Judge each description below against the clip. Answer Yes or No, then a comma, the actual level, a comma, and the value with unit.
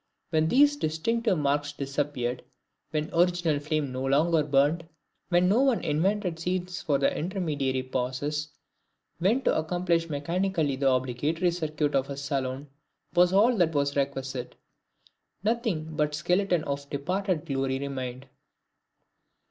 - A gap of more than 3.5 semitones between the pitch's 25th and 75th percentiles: Yes, average, 4.2 semitones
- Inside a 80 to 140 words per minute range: Yes, slow, 135 wpm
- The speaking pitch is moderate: Yes, medium, 155 Hz